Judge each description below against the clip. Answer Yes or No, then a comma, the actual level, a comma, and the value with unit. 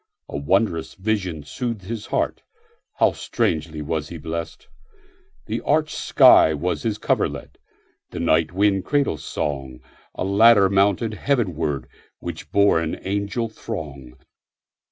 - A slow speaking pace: Yes, slow, 105 wpm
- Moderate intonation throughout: No, wide, 6.0 semitones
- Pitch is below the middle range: Yes, very low, 95 Hz